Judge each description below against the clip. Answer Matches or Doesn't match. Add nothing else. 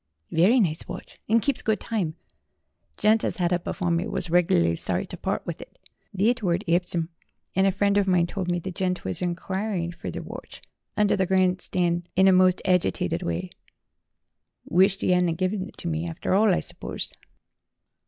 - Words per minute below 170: Doesn't match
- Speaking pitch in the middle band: Matches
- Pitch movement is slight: Matches